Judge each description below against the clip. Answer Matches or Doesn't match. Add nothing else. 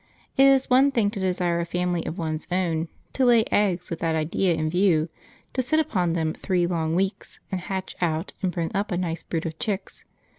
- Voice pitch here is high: Doesn't match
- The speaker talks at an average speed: Doesn't match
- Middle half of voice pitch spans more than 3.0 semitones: Matches